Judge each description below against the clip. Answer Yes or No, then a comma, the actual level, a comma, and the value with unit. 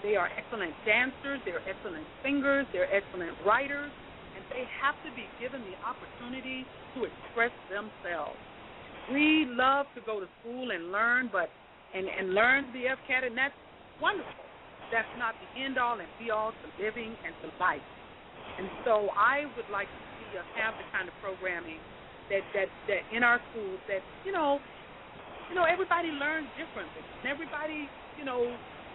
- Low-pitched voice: No, very high, 250 Hz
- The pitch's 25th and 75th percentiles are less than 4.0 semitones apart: No, average, 4.6 semitones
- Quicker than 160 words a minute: Yes, average, 170 wpm